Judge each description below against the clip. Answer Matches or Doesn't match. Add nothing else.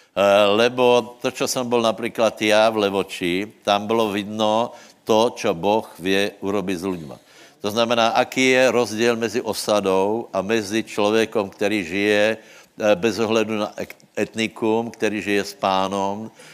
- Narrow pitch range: Matches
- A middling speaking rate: Matches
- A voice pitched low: Matches